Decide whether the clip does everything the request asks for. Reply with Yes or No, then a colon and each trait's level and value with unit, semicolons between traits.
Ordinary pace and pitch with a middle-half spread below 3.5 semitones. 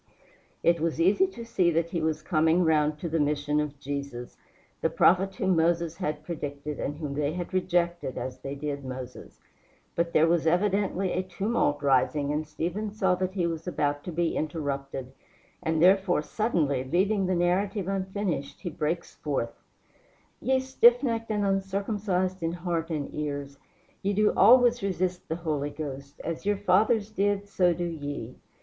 No: average, 165 wpm; average, 4.4 semitones